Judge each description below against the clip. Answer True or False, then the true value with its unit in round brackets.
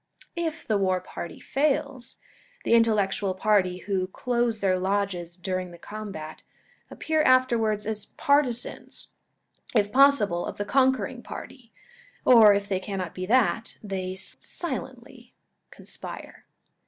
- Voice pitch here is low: False (215 Hz)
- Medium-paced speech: False (120 wpm)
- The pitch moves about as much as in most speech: True (5.0 semitones)